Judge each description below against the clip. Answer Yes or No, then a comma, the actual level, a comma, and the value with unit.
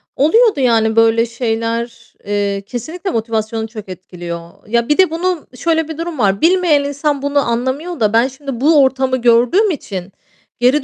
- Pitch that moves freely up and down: No, average, 5.0 semitones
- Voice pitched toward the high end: Yes, high, 245 Hz